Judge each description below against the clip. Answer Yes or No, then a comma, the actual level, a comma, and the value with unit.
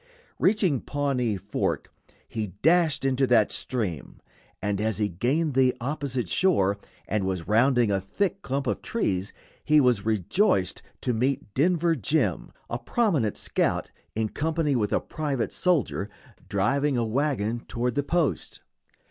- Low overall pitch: Yes, low, 125 Hz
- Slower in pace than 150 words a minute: Yes, average, 140 wpm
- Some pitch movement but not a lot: No, wide, 6.1 semitones